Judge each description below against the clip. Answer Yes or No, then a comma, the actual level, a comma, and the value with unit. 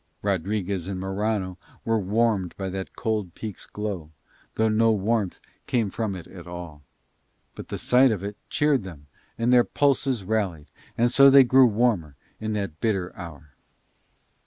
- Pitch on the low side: Yes, low, 105 Hz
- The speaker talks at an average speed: Yes, average, 160 wpm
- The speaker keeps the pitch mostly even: No, average, 3.8 semitones